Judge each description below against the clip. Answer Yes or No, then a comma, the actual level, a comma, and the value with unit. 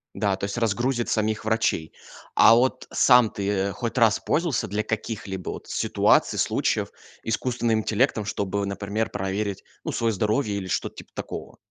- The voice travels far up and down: No, average, 2.7 semitones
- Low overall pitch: Yes, low, 110 Hz